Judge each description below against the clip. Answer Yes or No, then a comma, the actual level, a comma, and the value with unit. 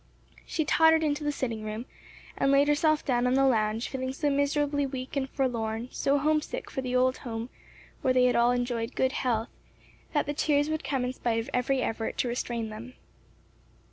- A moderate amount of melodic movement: Yes, average, 3.2 semitones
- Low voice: No, very high, 260 Hz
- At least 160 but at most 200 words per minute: Yes, average, 195 wpm